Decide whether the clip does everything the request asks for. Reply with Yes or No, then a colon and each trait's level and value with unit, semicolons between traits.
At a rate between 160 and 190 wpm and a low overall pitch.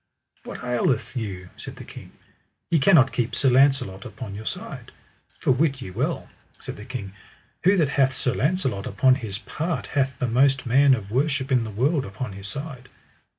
Yes: average, 185 wpm; low, 130 Hz